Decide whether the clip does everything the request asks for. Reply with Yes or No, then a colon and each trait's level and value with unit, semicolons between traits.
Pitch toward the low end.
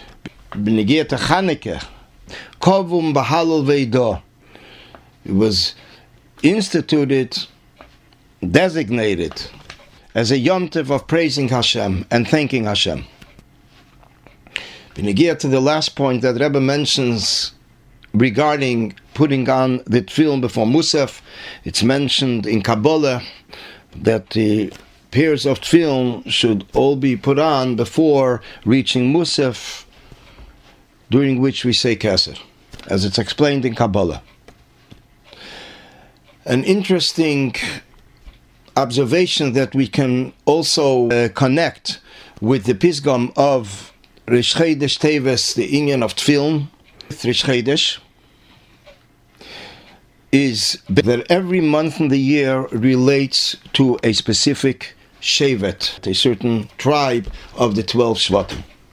Yes: low, 130 Hz